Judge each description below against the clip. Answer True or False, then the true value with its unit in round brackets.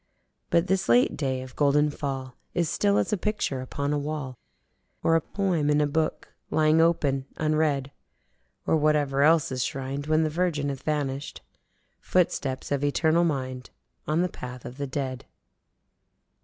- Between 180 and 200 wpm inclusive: False (160 wpm)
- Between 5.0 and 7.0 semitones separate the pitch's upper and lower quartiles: False (2.9 semitones)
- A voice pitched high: False (145 Hz)